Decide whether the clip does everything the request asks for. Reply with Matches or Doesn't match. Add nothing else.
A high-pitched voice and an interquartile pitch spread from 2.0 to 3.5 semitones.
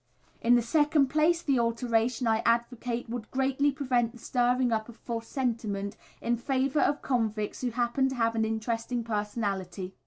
Matches